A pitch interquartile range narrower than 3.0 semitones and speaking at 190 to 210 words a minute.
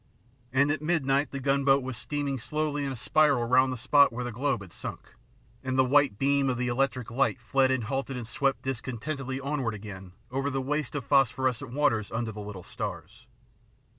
Yes: narrow, 2.5 semitones; average, 200 wpm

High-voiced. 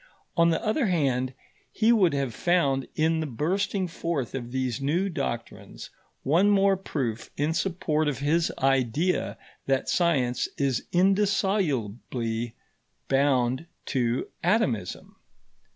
No: medium, 145 Hz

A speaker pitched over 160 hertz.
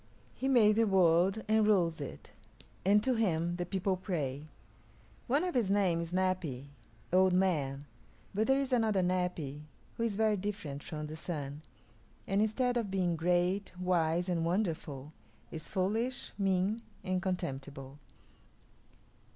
Yes: medium, 185 Hz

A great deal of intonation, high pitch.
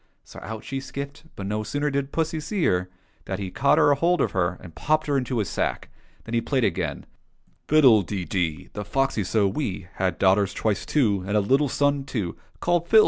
No: wide, 6.7 semitones; low, 115 Hz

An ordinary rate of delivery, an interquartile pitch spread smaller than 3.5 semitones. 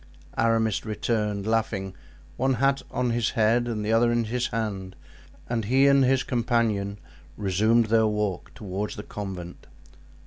Yes: average, 145 wpm; narrow, 2.4 semitones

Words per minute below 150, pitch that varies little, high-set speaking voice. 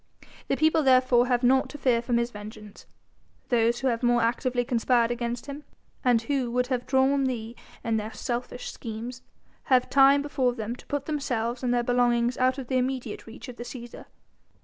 No: average, 190 wpm; narrow, 1.8 semitones; high, 245 Hz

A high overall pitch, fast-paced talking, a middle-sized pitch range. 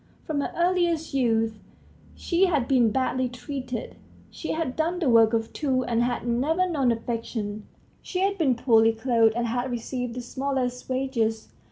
No: very high, 250 Hz; average, 165 wpm; average, 3.8 semitones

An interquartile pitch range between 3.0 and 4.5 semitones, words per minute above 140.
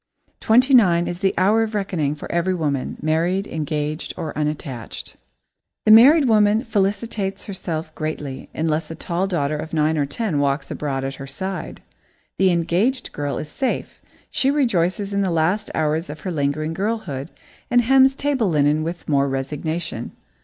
No: wide, 5.4 semitones; average, 160 wpm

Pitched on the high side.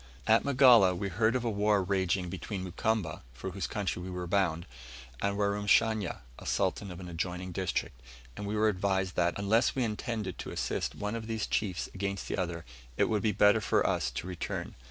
No: low, 100 Hz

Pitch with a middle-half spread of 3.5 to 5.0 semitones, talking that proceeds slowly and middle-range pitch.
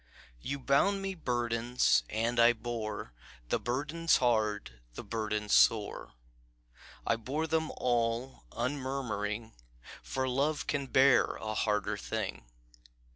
No: average, 4.0 semitones; slow, 115 wpm; low, 120 Hz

